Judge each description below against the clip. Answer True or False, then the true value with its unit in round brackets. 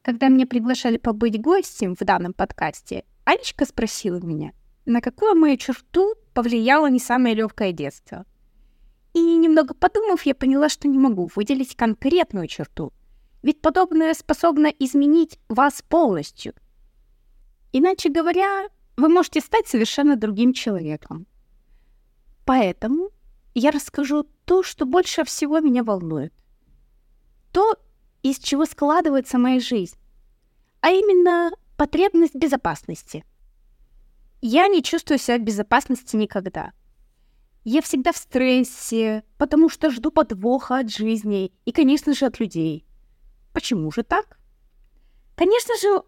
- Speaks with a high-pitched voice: True (275 Hz)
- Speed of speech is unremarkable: True (120 wpm)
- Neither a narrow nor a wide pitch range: False (6.1 semitones)